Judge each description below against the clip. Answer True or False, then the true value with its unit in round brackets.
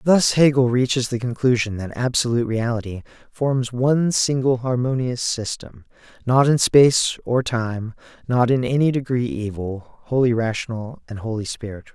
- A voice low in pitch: True (120 Hz)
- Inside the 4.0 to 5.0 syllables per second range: True (4.9 syllables/s)